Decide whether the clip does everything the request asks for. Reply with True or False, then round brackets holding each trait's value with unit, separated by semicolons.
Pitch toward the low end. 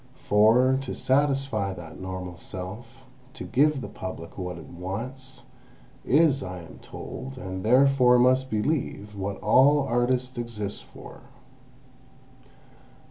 True (120 Hz)